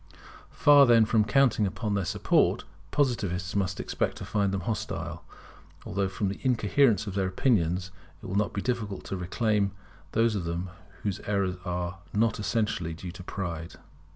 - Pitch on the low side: Yes, low, 100 Hz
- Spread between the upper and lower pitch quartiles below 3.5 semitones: Yes, average, 3.1 semitones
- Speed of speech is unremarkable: Yes, average, 165 wpm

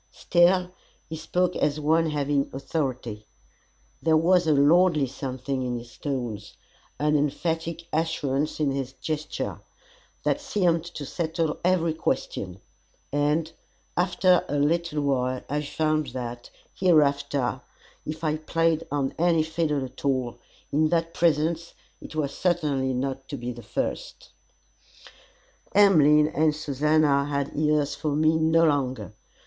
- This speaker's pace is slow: Yes, slow, 130 wpm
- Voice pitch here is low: No, medium, 150 Hz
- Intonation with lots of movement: No, average, 3.0 semitones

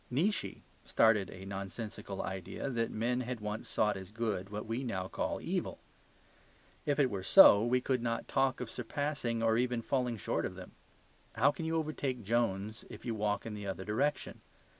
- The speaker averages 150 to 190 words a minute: Yes, average, 180 wpm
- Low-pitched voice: Yes, low, 115 Hz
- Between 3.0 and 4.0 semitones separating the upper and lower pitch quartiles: Yes, average, 3.5 semitones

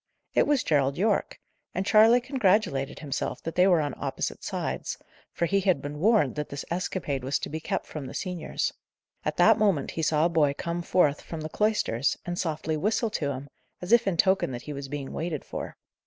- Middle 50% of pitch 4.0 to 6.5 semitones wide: Yes, average, 5.2 semitones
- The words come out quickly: Yes, fast, 210 wpm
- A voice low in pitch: No, medium, 165 Hz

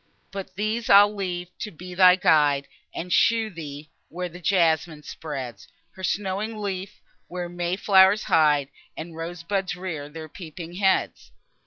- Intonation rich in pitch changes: No, average, 3.4 semitones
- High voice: No, medium, 180 Hz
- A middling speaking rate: Yes, average, 150 wpm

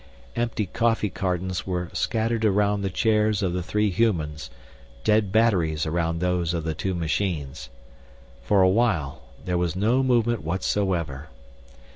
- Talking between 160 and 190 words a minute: No, average, 140 wpm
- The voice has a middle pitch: No, very low, 95 Hz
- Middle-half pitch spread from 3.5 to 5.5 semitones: Yes, average, 4.4 semitones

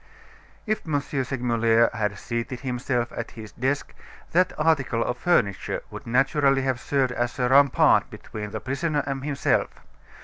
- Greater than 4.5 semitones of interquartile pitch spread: No, average, 3.2 semitones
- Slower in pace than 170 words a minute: Yes, average, 145 wpm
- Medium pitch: No, low, 130 Hz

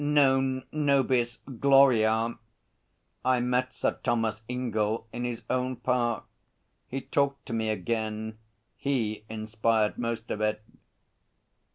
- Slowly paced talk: Yes, slow, 110 wpm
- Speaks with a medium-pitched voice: No, low, 120 Hz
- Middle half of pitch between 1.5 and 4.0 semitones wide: Yes, average, 2.8 semitones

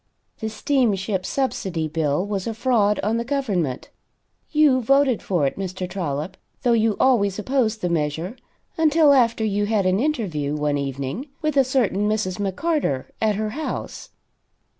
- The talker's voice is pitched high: Yes, high, 210 Hz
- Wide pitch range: Yes, wide, 6.1 semitones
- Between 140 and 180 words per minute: Yes, average, 155 wpm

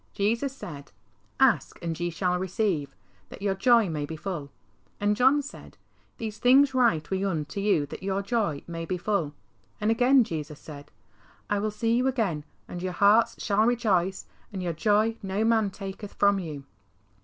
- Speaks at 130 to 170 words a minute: No, average, 180 wpm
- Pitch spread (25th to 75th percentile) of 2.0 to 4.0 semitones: No, average, 4.9 semitones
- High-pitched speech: Yes, high, 200 Hz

